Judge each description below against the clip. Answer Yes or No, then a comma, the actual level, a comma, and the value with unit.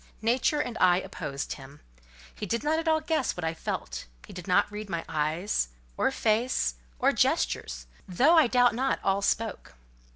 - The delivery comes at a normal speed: Yes, average, 175 wpm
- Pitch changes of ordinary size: No, wide, 7.5 semitones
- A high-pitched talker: Yes, high, 210 Hz